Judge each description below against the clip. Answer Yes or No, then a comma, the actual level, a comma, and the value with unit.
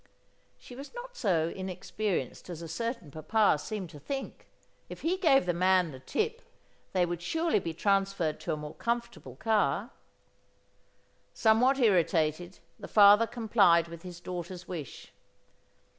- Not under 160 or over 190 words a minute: No, average, 145 wpm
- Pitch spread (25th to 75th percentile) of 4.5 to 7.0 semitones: Yes, wide, 5.5 semitones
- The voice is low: No, high, 190 Hz